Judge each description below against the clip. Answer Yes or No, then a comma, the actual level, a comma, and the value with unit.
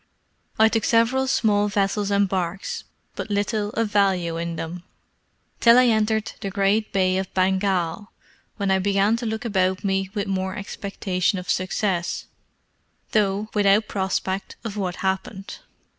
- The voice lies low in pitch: No, high, 200 Hz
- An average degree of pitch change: No, narrow, 2.1 semitones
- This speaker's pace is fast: No, average, 145 wpm